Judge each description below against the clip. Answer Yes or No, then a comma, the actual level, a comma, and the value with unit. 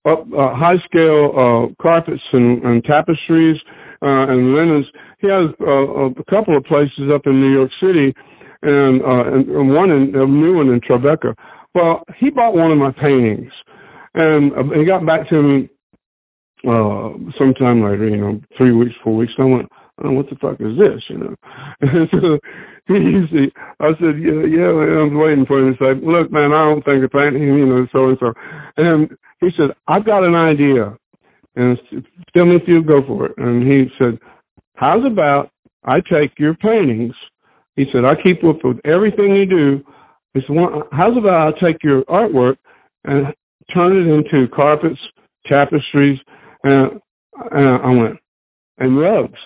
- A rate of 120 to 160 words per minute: No, average, 180 wpm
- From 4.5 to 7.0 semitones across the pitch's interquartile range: No, average, 3.7 semitones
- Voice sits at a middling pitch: Yes, medium, 145 Hz